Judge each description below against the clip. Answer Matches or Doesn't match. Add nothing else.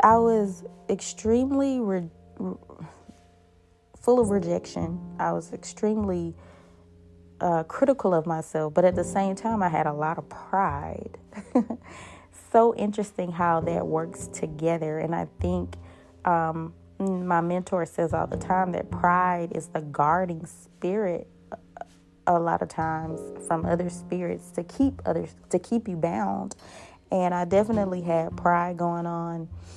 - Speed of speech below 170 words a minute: Matches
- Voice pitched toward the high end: Doesn't match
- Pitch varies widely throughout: Doesn't match